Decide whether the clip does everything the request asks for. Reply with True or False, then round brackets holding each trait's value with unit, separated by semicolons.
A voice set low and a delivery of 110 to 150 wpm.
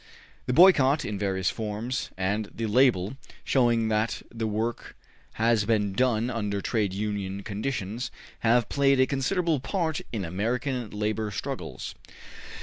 True (115 Hz; 135 wpm)